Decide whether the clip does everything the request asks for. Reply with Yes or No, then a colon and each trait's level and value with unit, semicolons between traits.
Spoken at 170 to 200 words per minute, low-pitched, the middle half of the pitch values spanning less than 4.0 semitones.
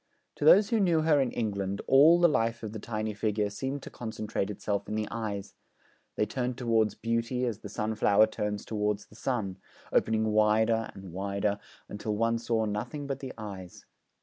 Yes: average, 180 wpm; low, 110 Hz; average, 2.9 semitones